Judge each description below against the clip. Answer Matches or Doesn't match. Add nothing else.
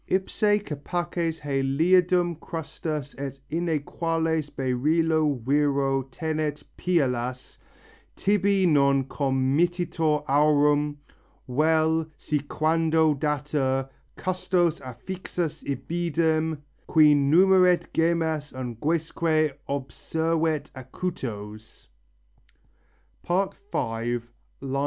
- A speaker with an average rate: Doesn't match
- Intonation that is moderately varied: Matches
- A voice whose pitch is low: Doesn't match